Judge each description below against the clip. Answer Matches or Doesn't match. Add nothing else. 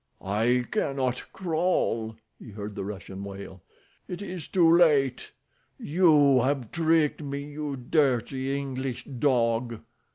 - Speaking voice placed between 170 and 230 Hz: Doesn't match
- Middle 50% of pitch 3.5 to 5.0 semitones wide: Matches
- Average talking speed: Doesn't match